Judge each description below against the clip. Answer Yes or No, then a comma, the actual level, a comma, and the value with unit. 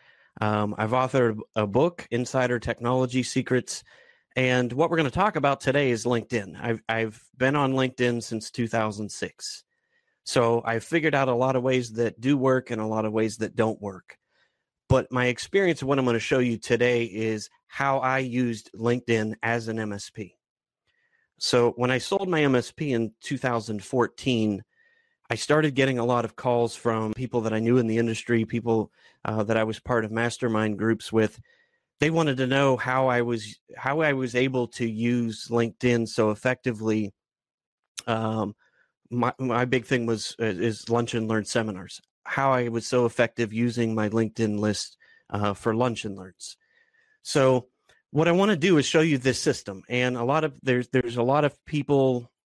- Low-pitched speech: Yes, low, 120 Hz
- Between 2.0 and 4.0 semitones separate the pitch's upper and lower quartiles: Yes, average, 2.8 semitones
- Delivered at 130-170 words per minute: No, average, 180 wpm